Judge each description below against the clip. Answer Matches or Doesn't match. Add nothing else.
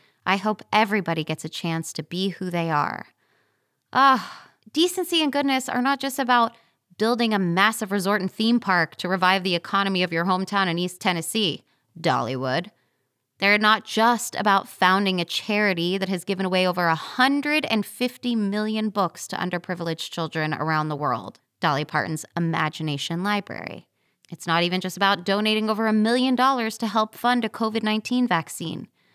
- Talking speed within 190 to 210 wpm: Doesn't match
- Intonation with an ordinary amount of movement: Matches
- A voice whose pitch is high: Matches